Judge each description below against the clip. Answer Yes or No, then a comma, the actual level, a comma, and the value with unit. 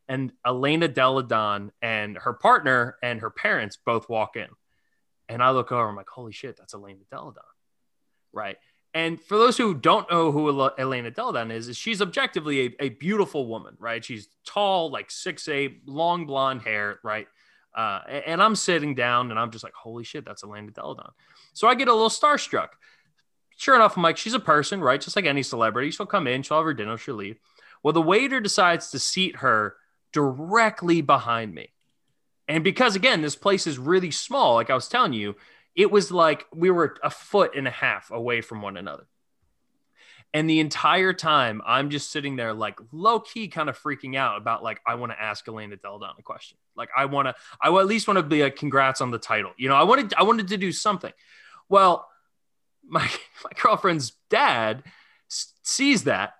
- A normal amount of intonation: No, wide, 8.0 semitones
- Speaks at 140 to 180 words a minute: No, average, 195 wpm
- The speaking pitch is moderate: Yes, medium, 150 Hz